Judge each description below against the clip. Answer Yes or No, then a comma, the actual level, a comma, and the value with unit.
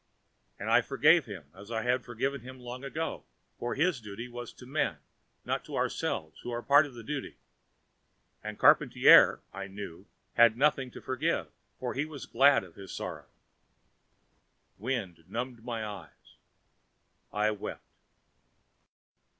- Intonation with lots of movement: No, average, 4.1 semitones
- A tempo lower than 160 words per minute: Yes, average, 150 wpm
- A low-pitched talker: Yes, low, 120 Hz